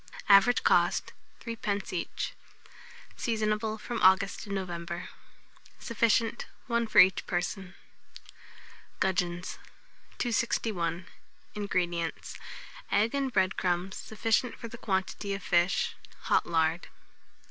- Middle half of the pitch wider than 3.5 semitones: Yes, average, 4.1 semitones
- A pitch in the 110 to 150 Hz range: No, high, 195 Hz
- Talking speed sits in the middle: No, slow, 100 wpm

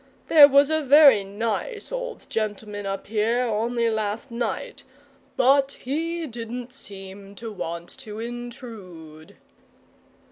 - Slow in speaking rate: Yes, slow, 115 wpm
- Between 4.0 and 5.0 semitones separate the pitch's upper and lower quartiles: Yes, average, 4.7 semitones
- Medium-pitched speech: No, high, 230 Hz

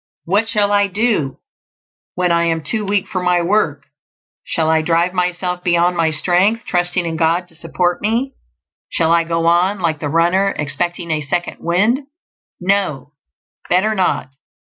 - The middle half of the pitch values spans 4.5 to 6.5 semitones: No, average, 2.9 semitones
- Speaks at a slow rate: No, average, 160 wpm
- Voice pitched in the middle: Yes, medium, 175 Hz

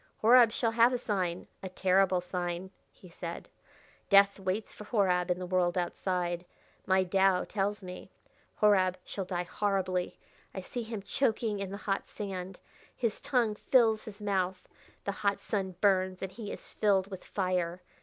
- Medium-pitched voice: No, high, 195 Hz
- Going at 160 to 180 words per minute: Yes, average, 165 wpm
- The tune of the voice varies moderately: No, narrow, 2.3 semitones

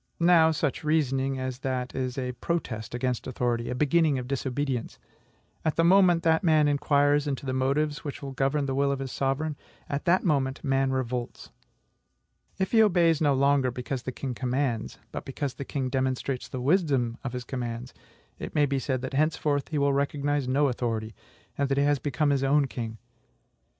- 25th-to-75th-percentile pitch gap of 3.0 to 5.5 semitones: No, narrow, 2.4 semitones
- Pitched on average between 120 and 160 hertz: Yes, low, 135 Hz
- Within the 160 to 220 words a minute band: Yes, average, 185 wpm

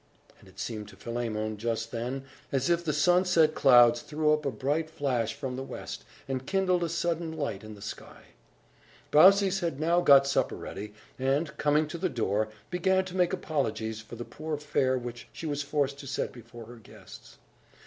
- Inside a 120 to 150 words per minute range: No, average, 190 wpm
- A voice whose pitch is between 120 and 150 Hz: Yes, medium, 140 Hz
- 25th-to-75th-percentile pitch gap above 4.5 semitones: Yes, wide, 5.5 semitones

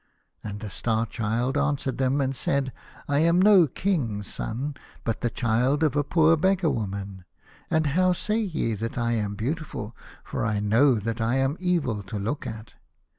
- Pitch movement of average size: No, wide, 5.7 semitones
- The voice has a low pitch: Yes, low, 130 Hz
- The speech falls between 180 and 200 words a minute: Yes, average, 185 wpm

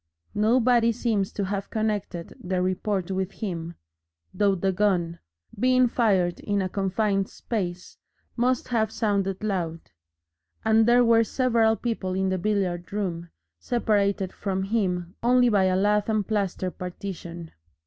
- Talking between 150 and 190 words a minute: No, average, 140 wpm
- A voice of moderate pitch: No, high, 200 Hz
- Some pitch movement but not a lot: Yes, average, 3.1 semitones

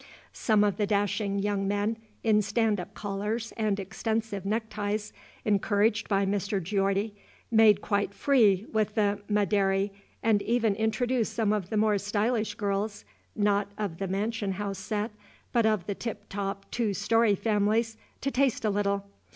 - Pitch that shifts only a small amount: Yes, narrow, 1.7 semitones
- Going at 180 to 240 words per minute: No, average, 155 wpm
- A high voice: Yes, high, 205 Hz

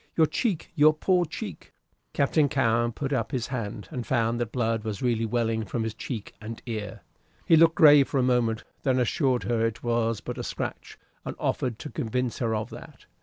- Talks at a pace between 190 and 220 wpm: Yes, average, 200 wpm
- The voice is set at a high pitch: No, low, 120 Hz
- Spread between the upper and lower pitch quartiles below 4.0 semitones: Yes, average, 3.3 semitones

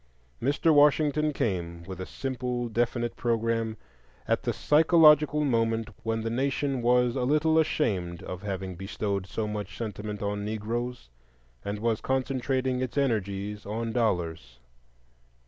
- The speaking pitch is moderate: No, low, 115 Hz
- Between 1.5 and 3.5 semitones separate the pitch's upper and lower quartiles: No, average, 4.3 semitones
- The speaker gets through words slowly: Yes, slow, 130 wpm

